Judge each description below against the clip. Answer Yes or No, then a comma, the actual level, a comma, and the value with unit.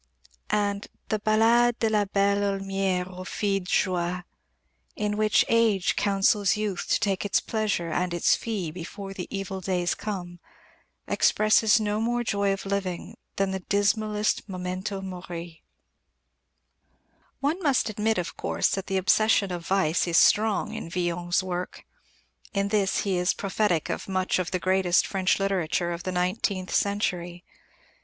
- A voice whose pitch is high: Yes, high, 195 Hz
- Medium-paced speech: Yes, average, 150 wpm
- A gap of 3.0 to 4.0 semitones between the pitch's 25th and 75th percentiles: No, narrow, 2.5 semitones